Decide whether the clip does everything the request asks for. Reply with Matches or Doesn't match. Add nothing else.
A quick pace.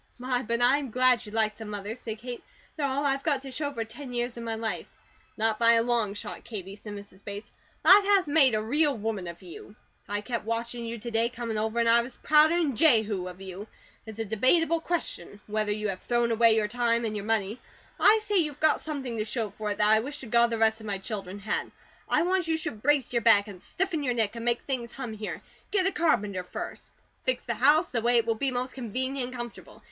Matches